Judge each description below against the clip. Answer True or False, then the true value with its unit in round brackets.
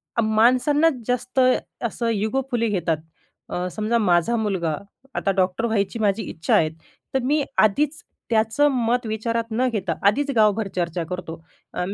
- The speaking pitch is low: False (220 Hz)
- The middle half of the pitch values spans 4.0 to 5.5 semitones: True (4.3 semitones)